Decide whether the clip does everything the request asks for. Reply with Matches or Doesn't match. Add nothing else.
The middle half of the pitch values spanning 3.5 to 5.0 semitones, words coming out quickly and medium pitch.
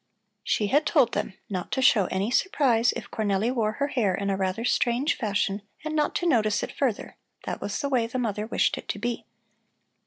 Doesn't match